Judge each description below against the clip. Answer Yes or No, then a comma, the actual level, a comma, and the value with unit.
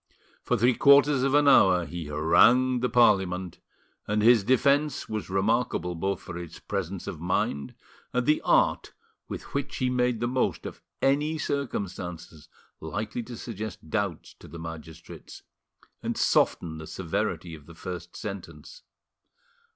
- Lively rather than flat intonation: Yes, wide, 6.6 semitones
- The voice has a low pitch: Yes, low, 100 Hz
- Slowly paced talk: No, average, 145 wpm